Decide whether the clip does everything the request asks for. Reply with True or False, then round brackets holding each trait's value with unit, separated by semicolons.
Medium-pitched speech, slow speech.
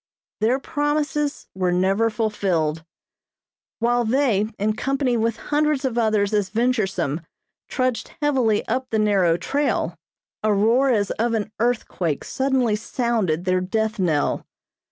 False (220 Hz; 130 wpm)